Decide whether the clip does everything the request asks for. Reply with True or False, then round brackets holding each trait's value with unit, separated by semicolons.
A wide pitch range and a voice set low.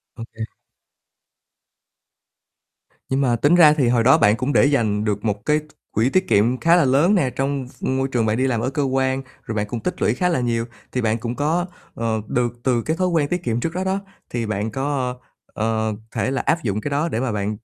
False (4.4 semitones; 130 Hz)